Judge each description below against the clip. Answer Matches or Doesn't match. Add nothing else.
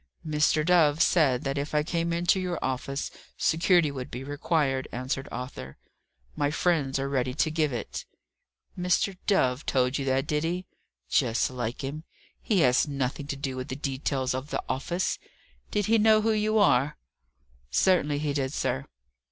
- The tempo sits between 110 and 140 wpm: Doesn't match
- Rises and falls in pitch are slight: Doesn't match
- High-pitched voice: Doesn't match